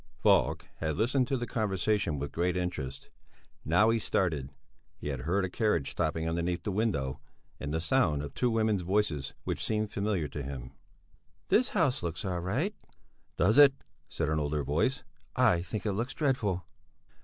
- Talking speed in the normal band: Yes, average, 170 wpm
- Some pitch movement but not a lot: No, wide, 6.2 semitones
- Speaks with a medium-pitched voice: No, very low, 90 Hz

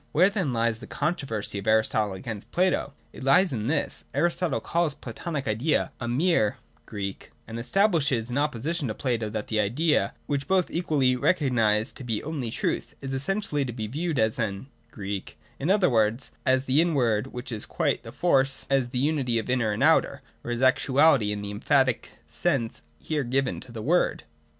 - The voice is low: Yes, low, 130 Hz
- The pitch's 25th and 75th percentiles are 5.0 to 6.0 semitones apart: Yes, wide, 5.4 semitones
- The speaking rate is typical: Yes, average, 195 wpm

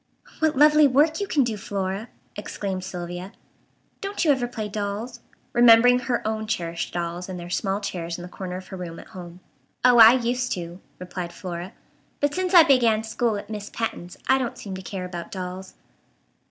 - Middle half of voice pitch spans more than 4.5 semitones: Yes, average, 5.2 semitones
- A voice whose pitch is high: Yes, high, 205 Hz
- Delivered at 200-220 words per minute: No, average, 190 wpm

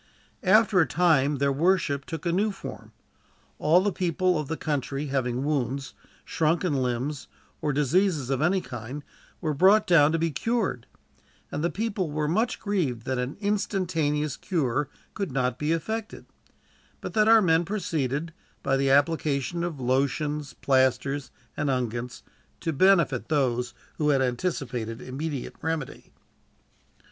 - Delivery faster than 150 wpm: No, average, 145 wpm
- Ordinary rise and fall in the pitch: Yes, average, 4.7 semitones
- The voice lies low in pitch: No, medium, 150 Hz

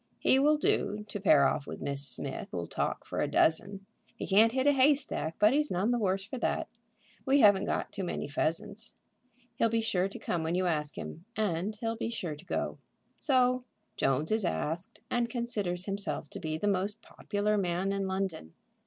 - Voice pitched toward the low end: No, high, 195 Hz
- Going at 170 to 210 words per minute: Yes, average, 200 wpm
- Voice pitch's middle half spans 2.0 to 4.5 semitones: No, average, 5.3 semitones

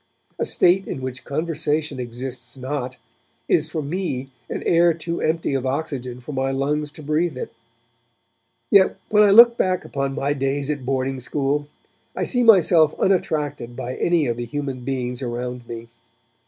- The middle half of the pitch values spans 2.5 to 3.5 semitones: No, average, 4.0 semitones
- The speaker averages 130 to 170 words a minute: Yes, average, 165 wpm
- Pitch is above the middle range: No, medium, 140 Hz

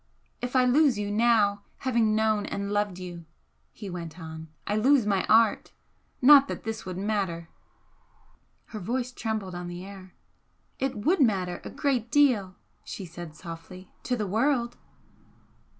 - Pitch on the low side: No, high, 210 Hz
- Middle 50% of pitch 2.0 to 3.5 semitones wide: No, average, 4.6 semitones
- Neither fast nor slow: Yes, average, 155 wpm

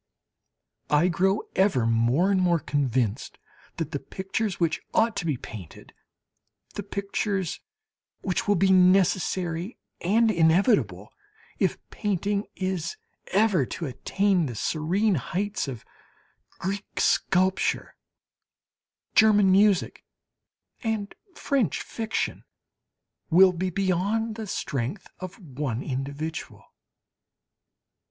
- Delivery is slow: Yes, slow, 105 wpm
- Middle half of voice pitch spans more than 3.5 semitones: Yes, average, 4.7 semitones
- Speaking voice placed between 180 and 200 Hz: Yes, medium, 185 Hz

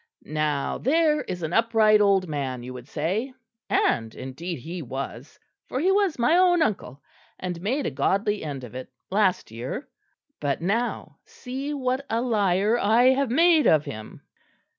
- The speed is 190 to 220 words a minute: No, average, 160 wpm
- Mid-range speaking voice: No, high, 200 Hz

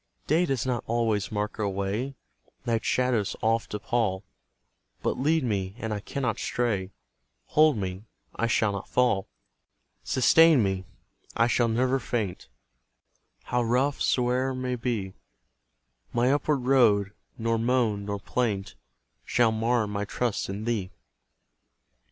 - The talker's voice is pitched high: No, low, 115 Hz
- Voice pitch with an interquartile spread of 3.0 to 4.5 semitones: Yes, average, 3.6 semitones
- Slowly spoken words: Yes, slow, 130 wpm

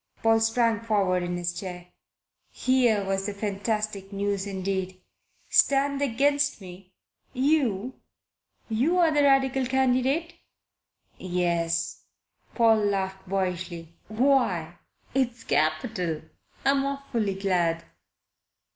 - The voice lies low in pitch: No, high, 210 Hz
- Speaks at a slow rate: Yes, slow, 95 wpm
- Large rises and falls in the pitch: Yes, wide, 5.9 semitones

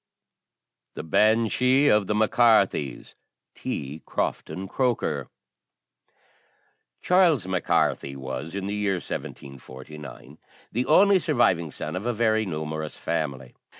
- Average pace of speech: No, slow, 115 wpm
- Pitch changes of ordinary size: No, wide, 7.3 semitones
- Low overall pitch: Yes, very low, 95 Hz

